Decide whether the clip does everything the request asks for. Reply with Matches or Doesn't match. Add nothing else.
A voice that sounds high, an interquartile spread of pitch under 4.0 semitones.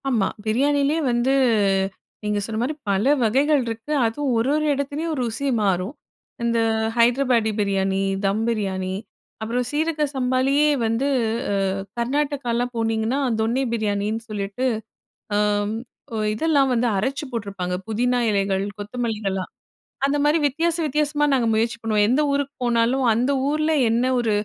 Doesn't match